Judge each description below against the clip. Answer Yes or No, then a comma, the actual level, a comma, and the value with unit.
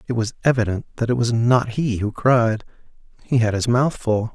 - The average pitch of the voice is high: No, low, 120 Hz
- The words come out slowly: No, fast, 205 wpm